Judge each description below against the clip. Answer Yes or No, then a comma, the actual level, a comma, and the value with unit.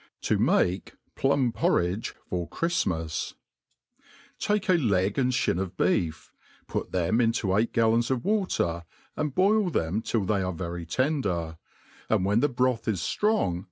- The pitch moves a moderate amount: No, wide, 7.2 semitones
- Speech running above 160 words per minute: No, average, 150 wpm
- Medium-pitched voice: No, low, 110 Hz